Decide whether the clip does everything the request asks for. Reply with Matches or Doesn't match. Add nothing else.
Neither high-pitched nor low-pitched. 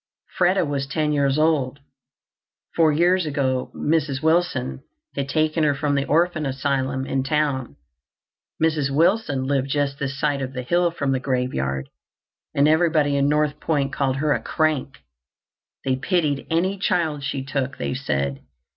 Matches